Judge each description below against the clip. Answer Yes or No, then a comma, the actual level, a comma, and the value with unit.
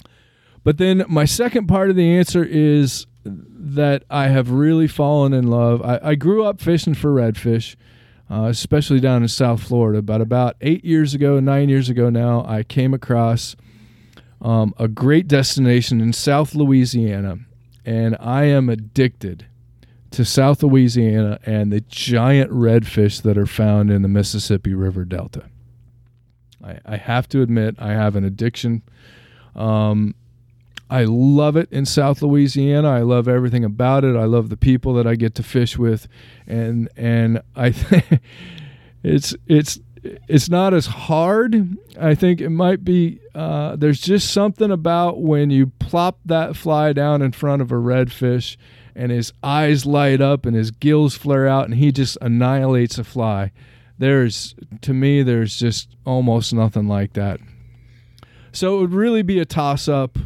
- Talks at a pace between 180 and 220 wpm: No, average, 160 wpm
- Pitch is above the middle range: No, low, 125 Hz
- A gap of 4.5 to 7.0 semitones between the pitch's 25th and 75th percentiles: No, average, 3.9 semitones